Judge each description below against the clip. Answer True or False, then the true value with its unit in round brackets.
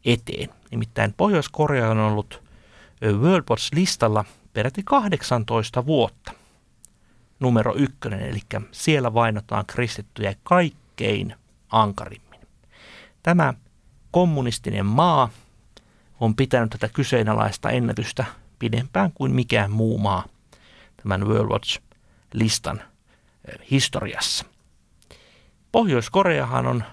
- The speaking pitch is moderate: False (115 Hz)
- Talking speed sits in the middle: False (80 wpm)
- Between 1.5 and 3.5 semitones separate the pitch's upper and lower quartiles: False (4.0 semitones)